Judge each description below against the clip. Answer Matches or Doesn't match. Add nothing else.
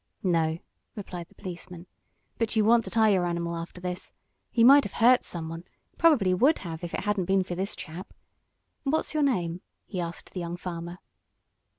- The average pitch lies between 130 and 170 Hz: Doesn't match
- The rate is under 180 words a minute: Doesn't match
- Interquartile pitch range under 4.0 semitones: Doesn't match